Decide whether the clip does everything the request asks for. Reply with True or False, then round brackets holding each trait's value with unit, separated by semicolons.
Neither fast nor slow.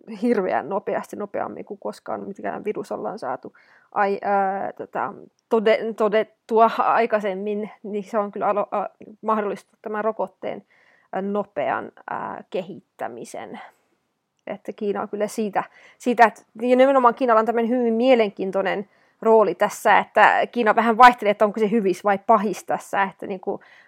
True (135 wpm)